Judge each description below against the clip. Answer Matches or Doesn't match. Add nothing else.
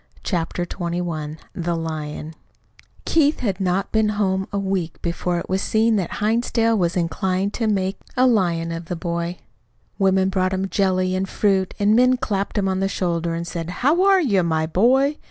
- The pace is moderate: Matches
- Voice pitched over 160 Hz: Matches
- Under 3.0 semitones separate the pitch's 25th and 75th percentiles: Doesn't match